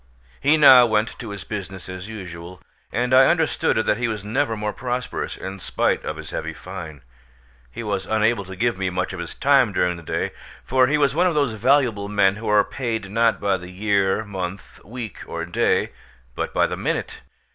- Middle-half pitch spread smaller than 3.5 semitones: No, average, 4.4 semitones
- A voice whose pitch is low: Yes, low, 105 Hz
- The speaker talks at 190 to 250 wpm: Yes, average, 200 wpm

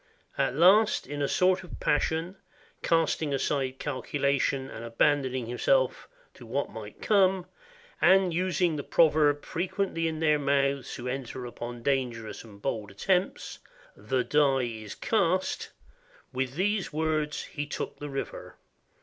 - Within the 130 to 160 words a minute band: Yes, average, 140 wpm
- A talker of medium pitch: Yes, medium, 145 Hz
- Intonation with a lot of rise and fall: No, average, 4.8 semitones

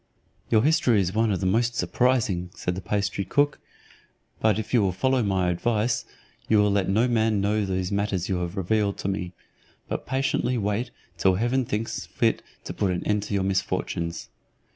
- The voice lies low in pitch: Yes, low, 105 Hz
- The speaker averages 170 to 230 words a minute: Yes, average, 185 wpm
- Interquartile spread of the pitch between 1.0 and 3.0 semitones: No, average, 3.4 semitones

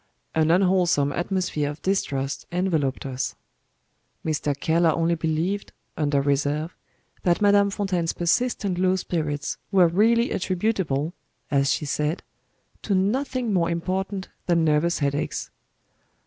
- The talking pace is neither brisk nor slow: No, slow, 120 wpm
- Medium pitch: Yes, medium, 170 Hz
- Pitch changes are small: No, average, 4.2 semitones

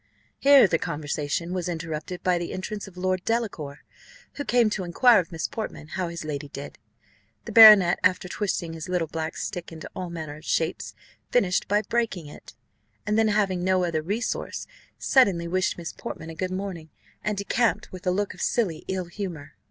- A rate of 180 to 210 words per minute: Yes, average, 185 wpm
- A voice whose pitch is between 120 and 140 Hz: No, medium, 180 Hz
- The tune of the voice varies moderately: Yes, average, 3.9 semitones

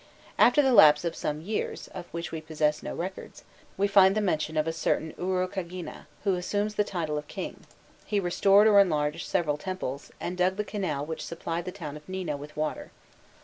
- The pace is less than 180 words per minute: No, average, 195 wpm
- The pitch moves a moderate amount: Yes, average, 4.0 semitones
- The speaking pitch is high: No, medium, 175 Hz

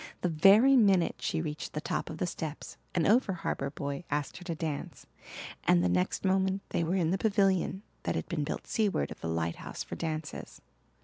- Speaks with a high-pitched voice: No, medium, 165 Hz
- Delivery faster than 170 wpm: Yes, average, 200 wpm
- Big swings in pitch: No, average, 4.5 semitones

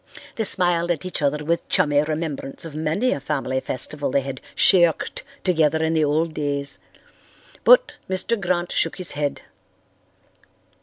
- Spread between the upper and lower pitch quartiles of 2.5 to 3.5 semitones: Yes, average, 3.2 semitones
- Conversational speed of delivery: Yes, average, 150 wpm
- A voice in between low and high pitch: Yes, medium, 160 Hz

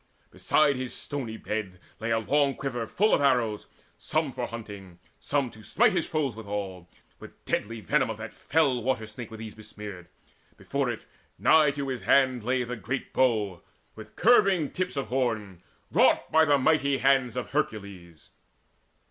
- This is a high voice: No, low, 120 Hz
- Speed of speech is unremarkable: Yes, average, 165 wpm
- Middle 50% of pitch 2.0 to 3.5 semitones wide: No, average, 4.5 semitones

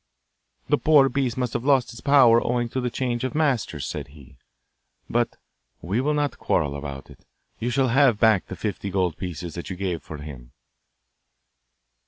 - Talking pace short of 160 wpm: No, average, 180 wpm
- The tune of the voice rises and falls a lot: Yes, wide, 8.0 semitones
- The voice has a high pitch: No, low, 115 Hz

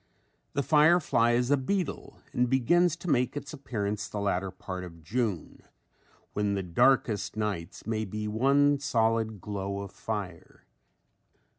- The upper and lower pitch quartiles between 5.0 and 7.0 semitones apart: Yes, average, 5.3 semitones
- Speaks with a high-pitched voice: No, low, 110 Hz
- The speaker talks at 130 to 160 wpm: Yes, average, 140 wpm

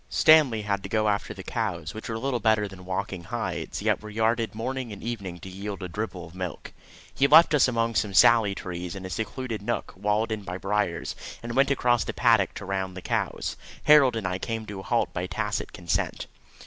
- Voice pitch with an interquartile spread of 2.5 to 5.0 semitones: Yes, average, 3.5 semitones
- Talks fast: Yes, fast, 215 wpm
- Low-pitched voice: Yes, low, 105 Hz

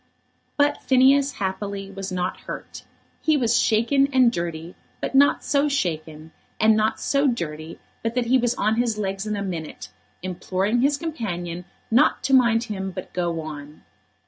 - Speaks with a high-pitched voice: Yes, high, 215 Hz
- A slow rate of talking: No, average, 165 wpm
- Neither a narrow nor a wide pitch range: No, wide, 6.3 semitones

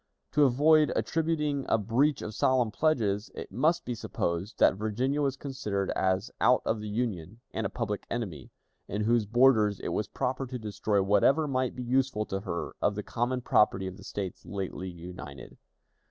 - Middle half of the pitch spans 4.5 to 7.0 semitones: Yes, average, 4.8 semitones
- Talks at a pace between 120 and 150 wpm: No, average, 180 wpm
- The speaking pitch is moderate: No, low, 115 Hz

